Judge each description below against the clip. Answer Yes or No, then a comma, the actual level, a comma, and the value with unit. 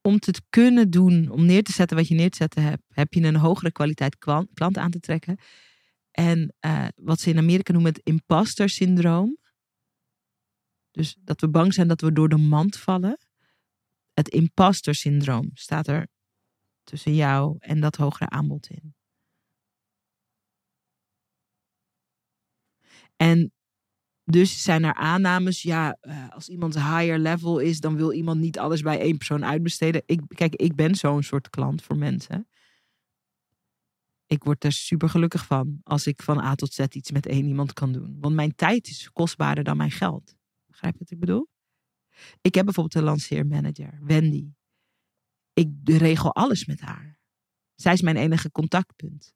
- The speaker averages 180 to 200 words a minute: No, average, 160 wpm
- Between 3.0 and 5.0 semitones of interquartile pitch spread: No, narrow, 2.6 semitones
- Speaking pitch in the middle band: Yes, medium, 160 Hz